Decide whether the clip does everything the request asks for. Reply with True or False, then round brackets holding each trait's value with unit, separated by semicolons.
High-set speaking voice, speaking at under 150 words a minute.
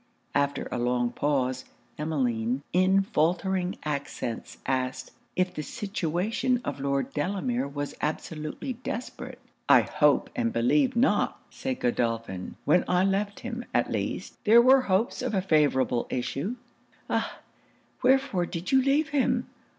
False (180 Hz; 135 wpm)